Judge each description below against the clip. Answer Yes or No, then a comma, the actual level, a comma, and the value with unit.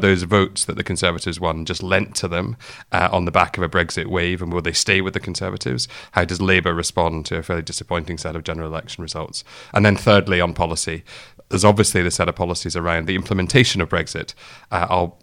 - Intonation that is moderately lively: No, narrow, 2.0 semitones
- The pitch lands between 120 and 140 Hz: No, very low, 90 Hz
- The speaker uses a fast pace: Yes, fast, 230 wpm